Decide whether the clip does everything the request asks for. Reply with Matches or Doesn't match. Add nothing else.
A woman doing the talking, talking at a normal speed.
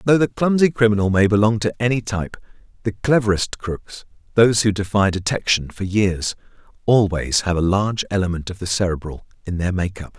Doesn't match